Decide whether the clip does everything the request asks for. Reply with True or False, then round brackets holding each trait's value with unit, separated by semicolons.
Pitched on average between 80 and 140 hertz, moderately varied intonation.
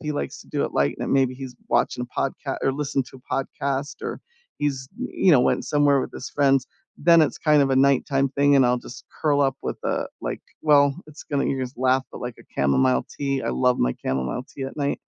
False (135 Hz; 2.2 semitones)